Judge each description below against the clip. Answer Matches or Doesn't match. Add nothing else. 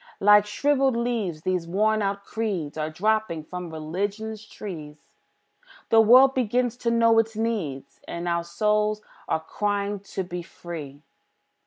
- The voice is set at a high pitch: Matches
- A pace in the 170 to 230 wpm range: Doesn't match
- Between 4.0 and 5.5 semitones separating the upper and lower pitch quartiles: Matches